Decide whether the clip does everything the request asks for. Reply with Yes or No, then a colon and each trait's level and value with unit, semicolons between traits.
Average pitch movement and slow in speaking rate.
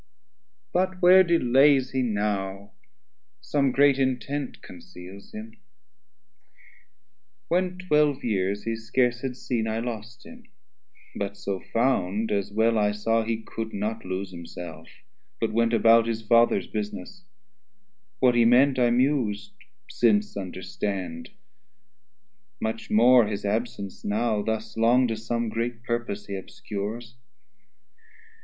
Yes: average, 3.6 semitones; slow, 125 wpm